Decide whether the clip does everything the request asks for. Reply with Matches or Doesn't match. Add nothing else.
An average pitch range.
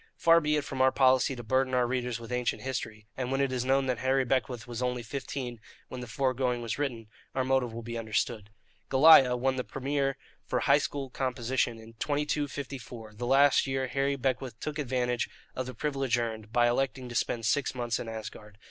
Doesn't match